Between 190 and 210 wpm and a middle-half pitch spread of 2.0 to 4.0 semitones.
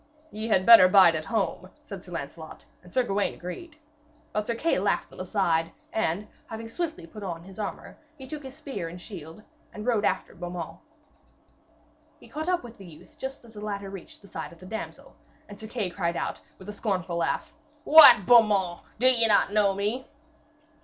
No: average, 195 wpm; average, 4.4 semitones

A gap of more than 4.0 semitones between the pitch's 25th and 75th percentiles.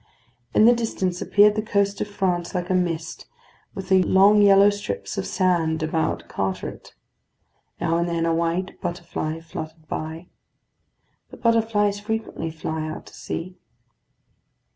No: average, 3.7 semitones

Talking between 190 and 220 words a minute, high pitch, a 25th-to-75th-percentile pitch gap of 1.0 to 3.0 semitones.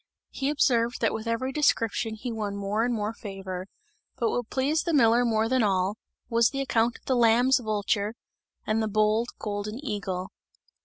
No: average, 175 wpm; high, 225 Hz; average, 2.7 semitones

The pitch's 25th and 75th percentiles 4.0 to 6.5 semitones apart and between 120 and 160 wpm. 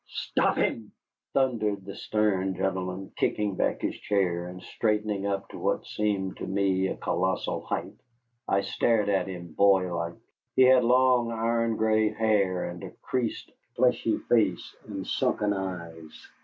No: average, 2.8 semitones; average, 145 wpm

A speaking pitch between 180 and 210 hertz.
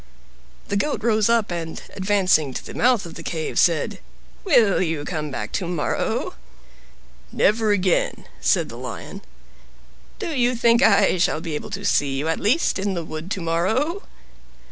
Yes: high, 190 Hz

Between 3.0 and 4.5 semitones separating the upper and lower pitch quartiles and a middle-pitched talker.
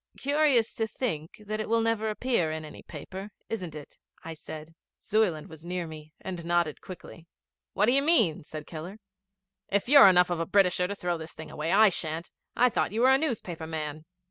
No: wide, 5.5 semitones; medium, 180 Hz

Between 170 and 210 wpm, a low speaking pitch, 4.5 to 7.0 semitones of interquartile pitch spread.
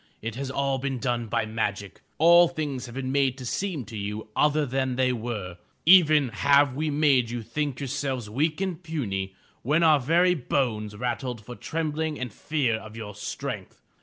Yes: average, 180 wpm; low, 130 Hz; average, 4.9 semitones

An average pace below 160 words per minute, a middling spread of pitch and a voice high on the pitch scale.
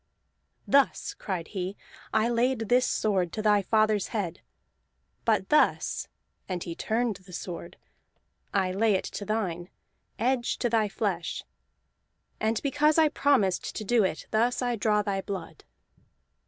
Yes: average, 140 wpm; average, 3.8 semitones; high, 215 Hz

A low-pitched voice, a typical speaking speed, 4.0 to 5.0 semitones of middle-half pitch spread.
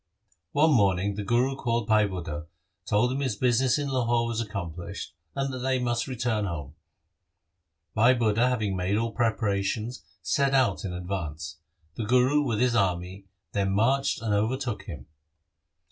Yes: low, 115 Hz; average, 150 wpm; average, 4.4 semitones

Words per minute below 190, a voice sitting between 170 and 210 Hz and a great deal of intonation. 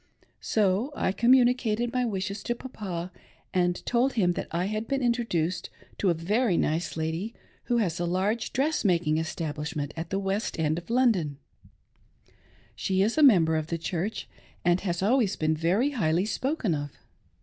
Yes: average, 160 wpm; high, 190 Hz; wide, 5.9 semitones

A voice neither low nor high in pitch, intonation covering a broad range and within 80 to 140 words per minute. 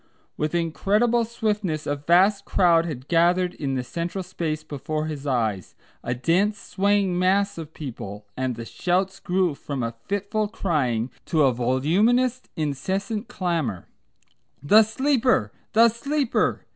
Yes: medium, 175 Hz; wide, 6.2 semitones; slow, 135 wpm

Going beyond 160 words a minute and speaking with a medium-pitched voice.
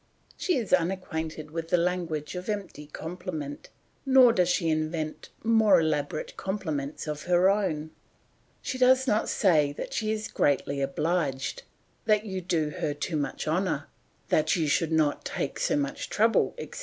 No: average, 155 wpm; medium, 170 Hz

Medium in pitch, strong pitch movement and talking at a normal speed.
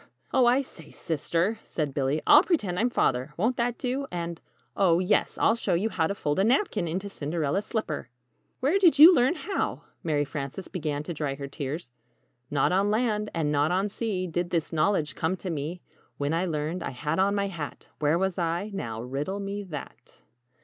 Yes: medium, 175 Hz; wide, 5.7 semitones; average, 195 wpm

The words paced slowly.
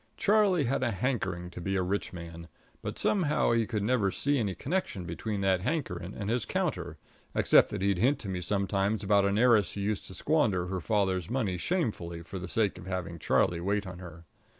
No: fast, 205 wpm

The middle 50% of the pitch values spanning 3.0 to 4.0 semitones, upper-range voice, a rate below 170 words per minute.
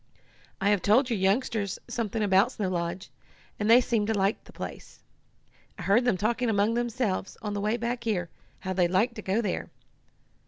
No: average, 3.4 semitones; high, 210 Hz; average, 190 wpm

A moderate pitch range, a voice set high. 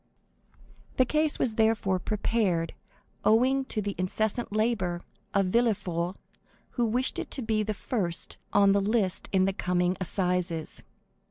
Yes: average, 3.7 semitones; high, 205 Hz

